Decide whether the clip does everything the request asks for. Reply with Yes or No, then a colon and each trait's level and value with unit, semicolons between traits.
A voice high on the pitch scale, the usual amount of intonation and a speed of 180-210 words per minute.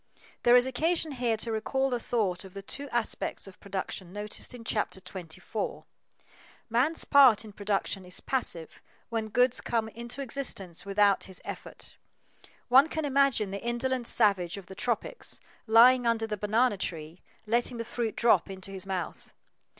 No: high, 225 Hz; average, 4.0 semitones; average, 160 wpm